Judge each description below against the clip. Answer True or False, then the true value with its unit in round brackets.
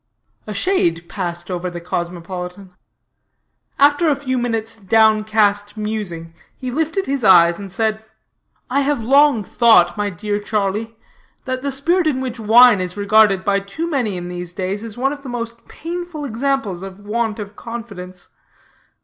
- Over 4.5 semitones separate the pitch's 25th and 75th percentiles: True (5.2 semitones)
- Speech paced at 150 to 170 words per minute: True (160 wpm)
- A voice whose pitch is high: True (215 Hz)